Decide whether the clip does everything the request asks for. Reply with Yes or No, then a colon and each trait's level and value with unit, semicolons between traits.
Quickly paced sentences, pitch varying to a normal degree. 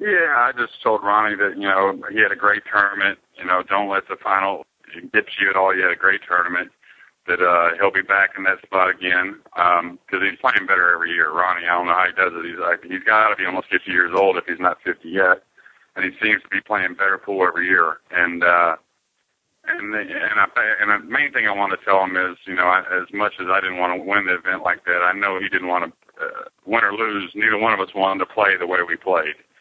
No: fast, 260 wpm; narrow, 2.2 semitones